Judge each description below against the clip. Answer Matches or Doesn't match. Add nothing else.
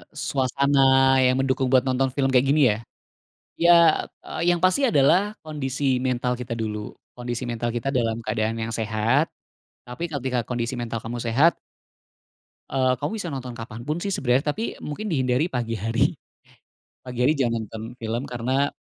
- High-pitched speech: Doesn't match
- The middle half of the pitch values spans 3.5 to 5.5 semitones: Doesn't match